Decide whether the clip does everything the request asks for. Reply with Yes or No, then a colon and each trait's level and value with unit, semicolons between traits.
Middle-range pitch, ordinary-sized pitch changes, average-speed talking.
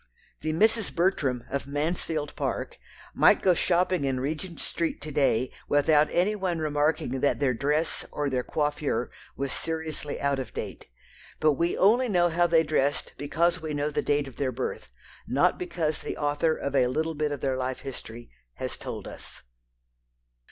Yes: medium, 150 Hz; average, 3.3 semitones; average, 170 wpm